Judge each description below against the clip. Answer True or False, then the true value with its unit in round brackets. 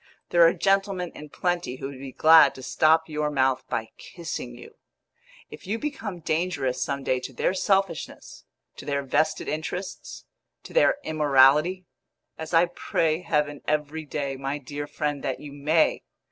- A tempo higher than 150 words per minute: True (160 wpm)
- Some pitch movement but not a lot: True (3.7 semitones)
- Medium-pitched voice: True (150 Hz)